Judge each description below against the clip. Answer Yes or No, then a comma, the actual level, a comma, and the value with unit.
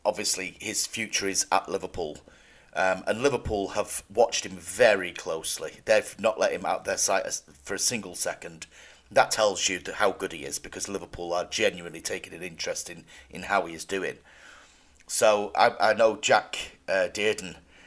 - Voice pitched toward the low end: Yes, very low, 95 Hz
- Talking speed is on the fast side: No, average, 180 wpm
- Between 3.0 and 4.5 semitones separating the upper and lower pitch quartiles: No, narrow, 2.6 semitones